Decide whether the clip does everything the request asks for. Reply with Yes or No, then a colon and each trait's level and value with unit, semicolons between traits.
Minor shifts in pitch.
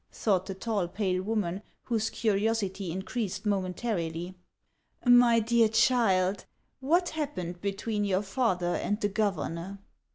No: average, 3.5 semitones